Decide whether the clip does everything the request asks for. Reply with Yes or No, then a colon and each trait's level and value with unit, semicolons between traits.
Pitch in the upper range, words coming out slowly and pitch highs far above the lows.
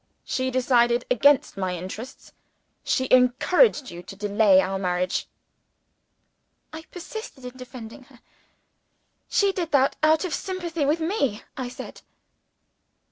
Yes: very high, 255 Hz; slow, 125 wpm; wide, 6.2 semitones